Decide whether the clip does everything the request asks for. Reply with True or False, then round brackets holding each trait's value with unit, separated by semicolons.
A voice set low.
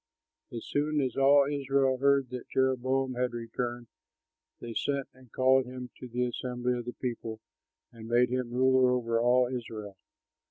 True (125 Hz)